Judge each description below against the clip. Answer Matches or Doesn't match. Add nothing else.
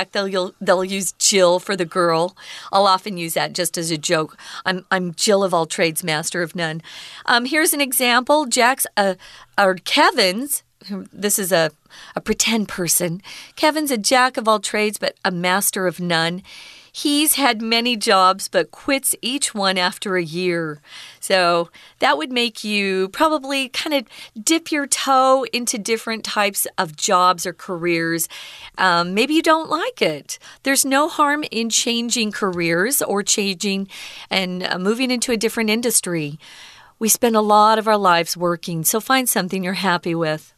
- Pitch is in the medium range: Doesn't match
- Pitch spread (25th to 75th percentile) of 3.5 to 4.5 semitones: Doesn't match